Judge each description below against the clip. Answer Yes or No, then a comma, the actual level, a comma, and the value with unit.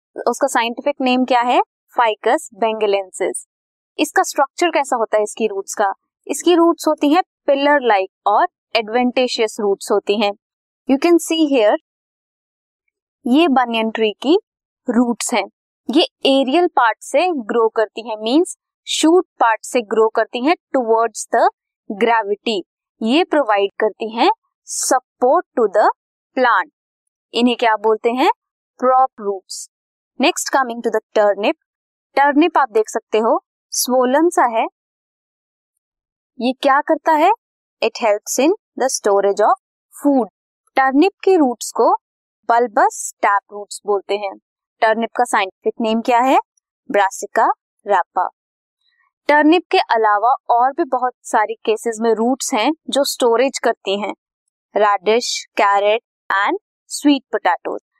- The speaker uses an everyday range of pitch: No, wide, 6.7 semitones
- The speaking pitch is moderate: No, very high, 255 Hz